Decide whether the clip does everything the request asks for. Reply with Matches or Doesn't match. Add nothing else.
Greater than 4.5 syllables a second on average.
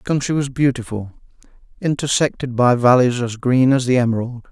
Matches